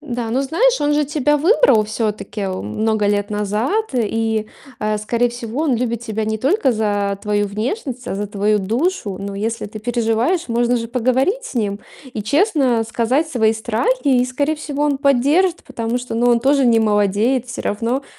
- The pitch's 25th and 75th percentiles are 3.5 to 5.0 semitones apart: Yes, average, 4.5 semitones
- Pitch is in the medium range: No, high, 235 Hz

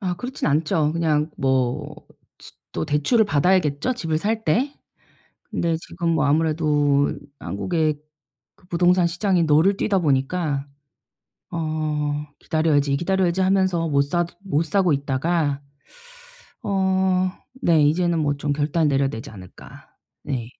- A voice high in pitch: No, medium, 160 Hz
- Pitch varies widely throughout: No, average, 3.8 semitones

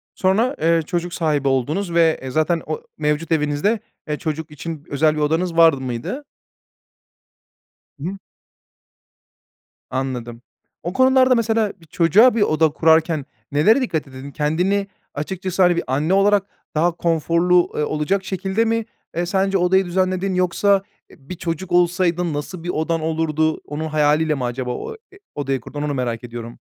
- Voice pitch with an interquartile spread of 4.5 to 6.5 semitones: No, average, 4.0 semitones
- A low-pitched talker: No, medium, 165 Hz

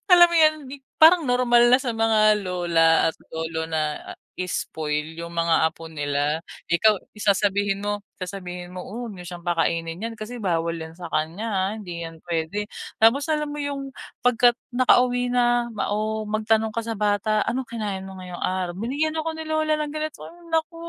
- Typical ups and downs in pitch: No, wide, 6.3 semitones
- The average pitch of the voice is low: No, high, 210 Hz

